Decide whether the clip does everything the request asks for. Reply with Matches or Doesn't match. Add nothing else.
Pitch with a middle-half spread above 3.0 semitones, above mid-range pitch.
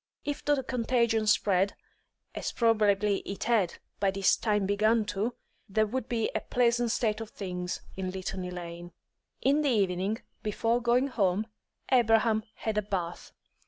Matches